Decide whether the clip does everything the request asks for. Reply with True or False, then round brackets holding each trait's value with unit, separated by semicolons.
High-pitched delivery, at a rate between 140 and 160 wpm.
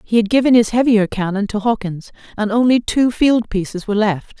False (220 Hz; 205 wpm)